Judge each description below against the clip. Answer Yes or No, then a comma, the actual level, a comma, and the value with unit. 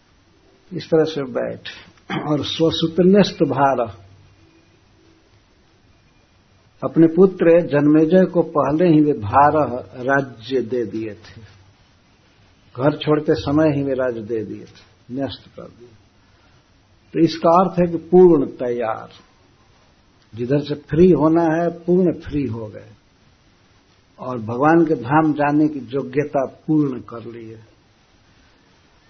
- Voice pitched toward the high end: No, low, 135 Hz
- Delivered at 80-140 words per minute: Yes, average, 120 wpm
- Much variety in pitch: Yes, wide, 6.5 semitones